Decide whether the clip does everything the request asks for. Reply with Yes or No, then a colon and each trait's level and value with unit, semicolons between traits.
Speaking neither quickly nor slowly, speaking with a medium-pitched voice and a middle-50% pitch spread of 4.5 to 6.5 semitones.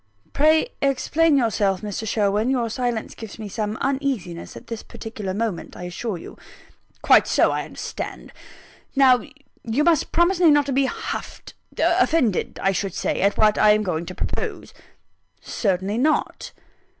No: average, 155 wpm; high, 225 Hz; wide, 5.4 semitones